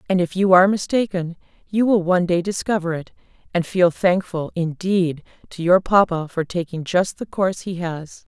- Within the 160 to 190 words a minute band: Yes, average, 180 wpm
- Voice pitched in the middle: Yes, medium, 180 Hz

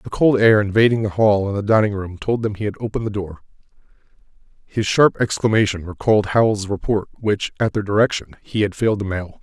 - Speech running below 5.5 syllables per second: No, 6.2 syllables/s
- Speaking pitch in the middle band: No, low, 105 Hz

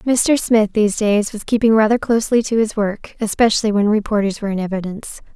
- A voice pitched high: Yes, high, 215 Hz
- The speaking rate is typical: Yes, average, 190 wpm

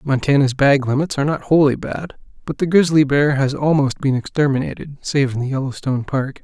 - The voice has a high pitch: No, medium, 140 Hz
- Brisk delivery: No, average, 185 wpm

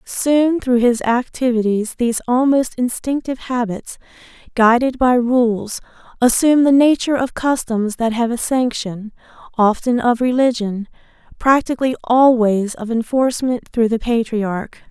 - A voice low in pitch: No, high, 240 Hz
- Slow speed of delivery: Yes, slow, 120 wpm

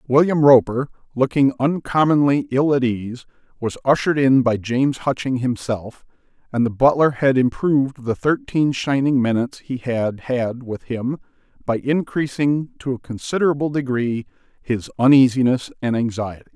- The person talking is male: Yes, male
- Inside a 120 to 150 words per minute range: Yes, average, 140 wpm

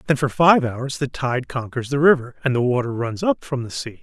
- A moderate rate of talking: No, fast, 255 wpm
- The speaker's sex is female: No, male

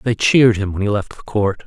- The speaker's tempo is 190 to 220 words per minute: No, fast, 290 wpm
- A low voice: Yes, low, 105 Hz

